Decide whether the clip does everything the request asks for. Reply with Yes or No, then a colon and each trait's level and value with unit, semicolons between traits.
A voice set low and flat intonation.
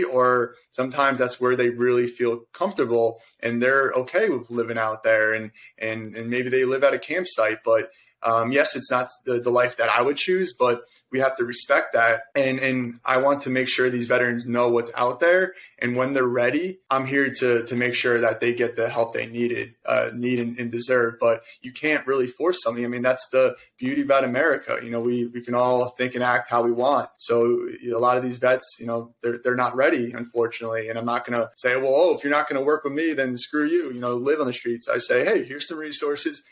Yes: low, 125 Hz; narrow, 2.1 semitones